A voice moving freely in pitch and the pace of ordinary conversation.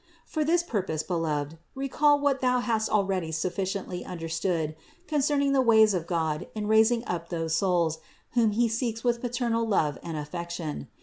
Yes: wide, 6.7 semitones; average, 170 wpm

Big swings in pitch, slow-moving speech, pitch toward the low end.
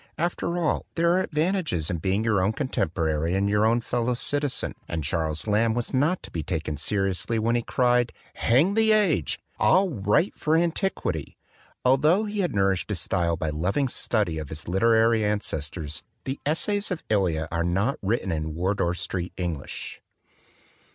No: wide, 9.0 semitones; average, 175 wpm; low, 105 Hz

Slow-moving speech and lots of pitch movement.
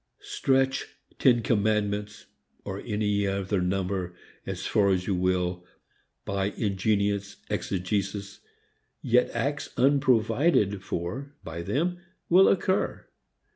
No: slow, 100 wpm; average, 4.1 semitones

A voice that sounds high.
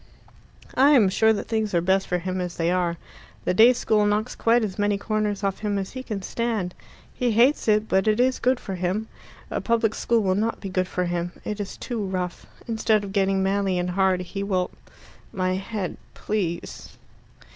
Yes: high, 200 Hz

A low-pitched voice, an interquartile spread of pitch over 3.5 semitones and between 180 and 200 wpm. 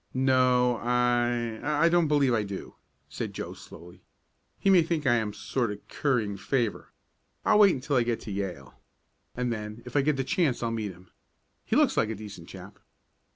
Yes: low, 120 Hz; average, 4.3 semitones; average, 190 wpm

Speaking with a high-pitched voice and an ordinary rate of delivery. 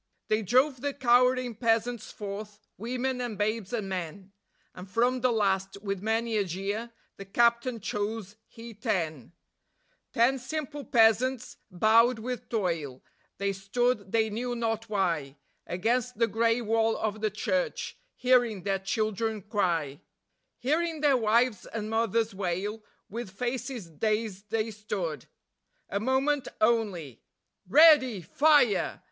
No: high, 220 Hz; slow, 130 wpm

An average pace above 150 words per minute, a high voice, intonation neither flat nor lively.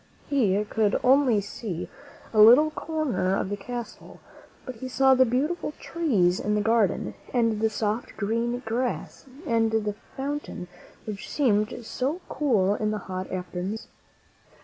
No: average, 145 wpm; high, 225 Hz; average, 3.9 semitones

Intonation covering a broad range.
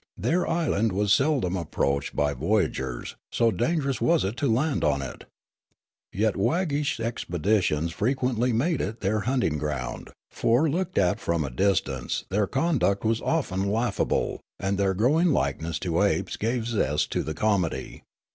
Yes: wide, 7.3 semitones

